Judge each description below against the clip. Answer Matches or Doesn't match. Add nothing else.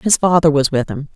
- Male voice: Doesn't match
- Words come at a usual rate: Doesn't match